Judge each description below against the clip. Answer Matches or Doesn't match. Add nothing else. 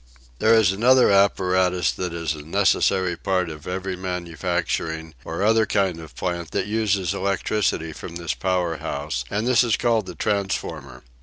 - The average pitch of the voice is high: Doesn't match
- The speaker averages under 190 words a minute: Matches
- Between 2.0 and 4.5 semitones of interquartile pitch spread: Matches